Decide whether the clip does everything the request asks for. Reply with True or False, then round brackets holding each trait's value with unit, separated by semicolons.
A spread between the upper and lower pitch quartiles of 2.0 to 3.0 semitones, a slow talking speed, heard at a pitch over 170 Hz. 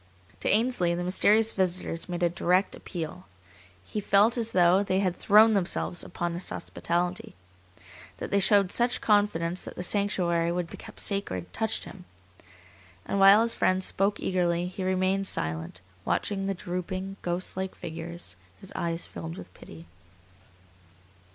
False (2.5 semitones; 150 wpm; 185 Hz)